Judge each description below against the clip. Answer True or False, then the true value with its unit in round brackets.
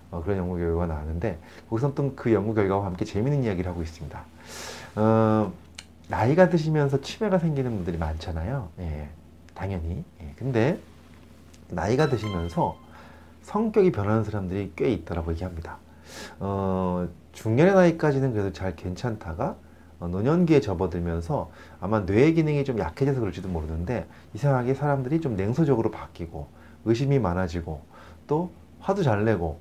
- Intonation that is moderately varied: False (7.6 semitones)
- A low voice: True (95 Hz)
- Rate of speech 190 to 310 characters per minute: False (345 characters per minute)